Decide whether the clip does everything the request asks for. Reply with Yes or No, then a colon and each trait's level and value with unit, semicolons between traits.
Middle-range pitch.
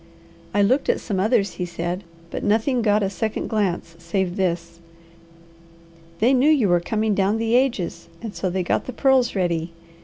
No: high, 200 Hz